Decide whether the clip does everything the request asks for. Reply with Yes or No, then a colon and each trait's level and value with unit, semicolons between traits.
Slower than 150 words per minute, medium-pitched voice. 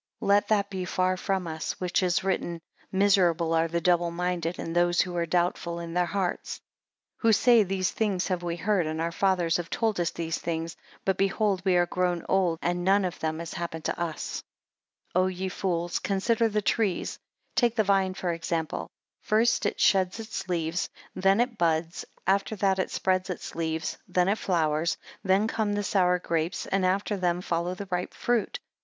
No: average, 200 wpm; medium, 180 Hz